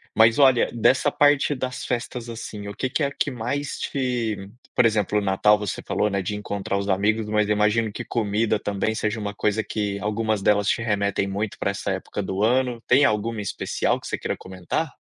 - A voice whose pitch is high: No, low, 105 Hz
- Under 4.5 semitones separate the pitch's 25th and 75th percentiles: Yes, narrow, 2.6 semitones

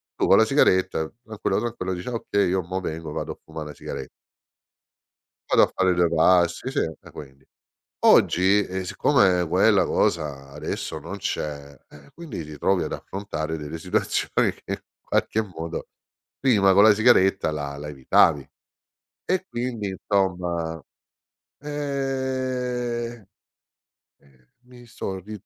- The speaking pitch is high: No, very low, 90 Hz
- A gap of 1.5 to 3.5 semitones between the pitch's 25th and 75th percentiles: No, average, 4.7 semitones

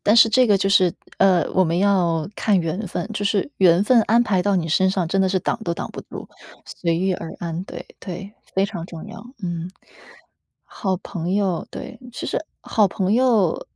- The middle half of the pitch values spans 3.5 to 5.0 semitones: No, average, 2.8 semitones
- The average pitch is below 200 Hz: Yes, high, 190 Hz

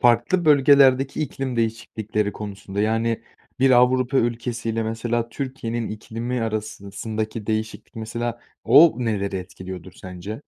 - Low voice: Yes, low, 115 Hz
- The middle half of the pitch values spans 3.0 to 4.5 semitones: No, narrow, 2.5 semitones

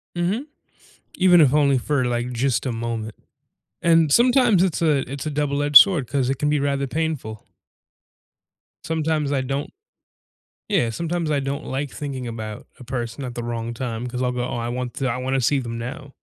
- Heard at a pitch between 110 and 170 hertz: Yes, low, 135 Hz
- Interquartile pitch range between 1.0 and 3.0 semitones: No, average, 3.8 semitones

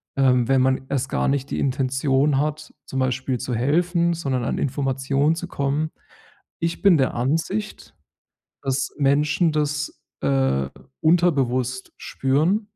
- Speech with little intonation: No, average, 3.0 semitones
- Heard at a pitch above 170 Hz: No, medium, 140 Hz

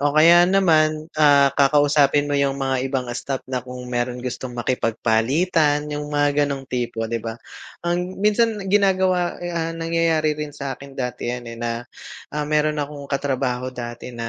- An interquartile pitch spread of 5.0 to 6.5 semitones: No, average, 3.7 semitones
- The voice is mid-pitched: Yes, medium, 145 Hz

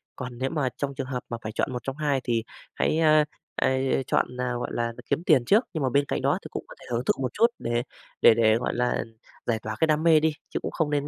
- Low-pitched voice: Yes, low, 130 Hz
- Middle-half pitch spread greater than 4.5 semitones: No, average, 4.1 semitones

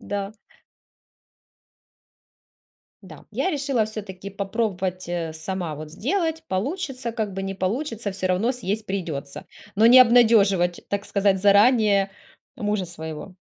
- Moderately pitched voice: No, high, 200 Hz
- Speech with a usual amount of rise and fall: Yes, average, 3.9 semitones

